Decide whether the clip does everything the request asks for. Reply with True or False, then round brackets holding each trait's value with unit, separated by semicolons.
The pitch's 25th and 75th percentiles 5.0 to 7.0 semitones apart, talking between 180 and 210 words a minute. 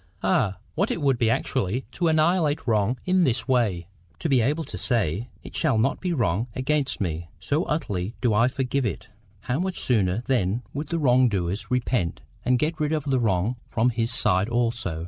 True (5.5 semitones; 190 wpm)